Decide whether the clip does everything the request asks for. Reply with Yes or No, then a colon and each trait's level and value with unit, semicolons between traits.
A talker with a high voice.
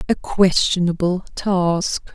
No: medium, 180 Hz